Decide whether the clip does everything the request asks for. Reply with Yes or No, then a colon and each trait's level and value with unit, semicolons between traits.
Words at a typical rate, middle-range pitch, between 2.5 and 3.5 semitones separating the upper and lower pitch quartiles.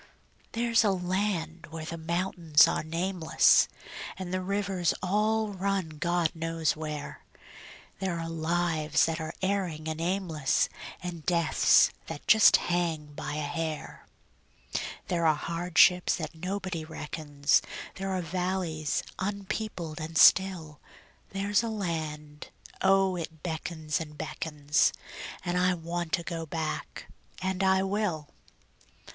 No: slow, 125 wpm; medium, 170 Hz; average, 3.1 semitones